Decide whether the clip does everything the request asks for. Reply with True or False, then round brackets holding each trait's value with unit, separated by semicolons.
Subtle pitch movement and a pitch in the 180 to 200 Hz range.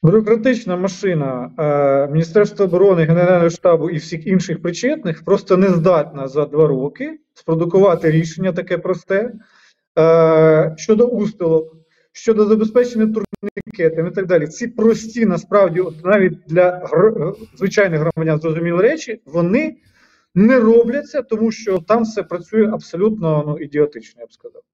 False (5.1 semitones; 185 Hz)